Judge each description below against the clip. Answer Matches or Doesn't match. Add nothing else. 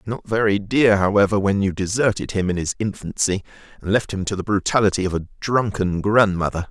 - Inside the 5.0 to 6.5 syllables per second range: Matches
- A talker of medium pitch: Doesn't match